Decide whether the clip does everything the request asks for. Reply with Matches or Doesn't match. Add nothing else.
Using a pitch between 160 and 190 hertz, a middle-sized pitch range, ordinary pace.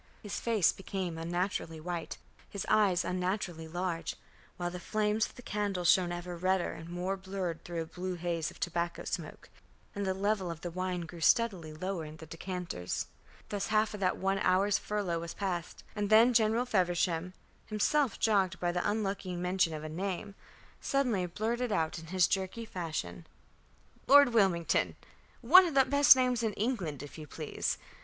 Matches